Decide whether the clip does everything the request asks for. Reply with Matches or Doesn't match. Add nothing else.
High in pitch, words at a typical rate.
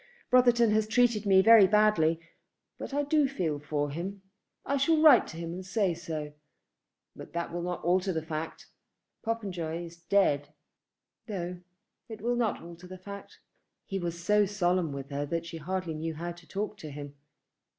Doesn't match